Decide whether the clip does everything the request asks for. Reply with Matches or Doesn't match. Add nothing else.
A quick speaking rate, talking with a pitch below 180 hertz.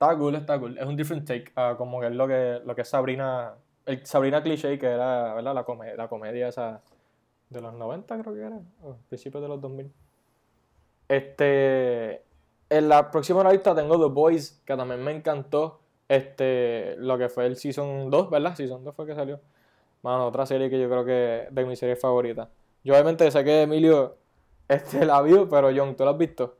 Matches